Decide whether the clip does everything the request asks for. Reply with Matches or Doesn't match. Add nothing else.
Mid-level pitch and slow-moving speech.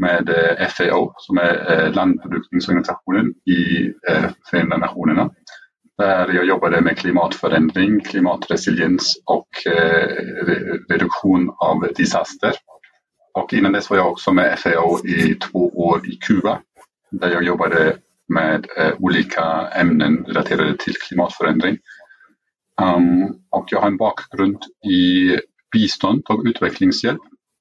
Doesn't match